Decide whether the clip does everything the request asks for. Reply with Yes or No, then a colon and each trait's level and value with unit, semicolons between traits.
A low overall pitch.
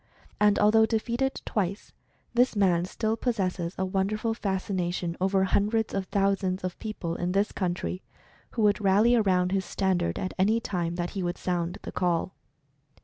No: high, 195 Hz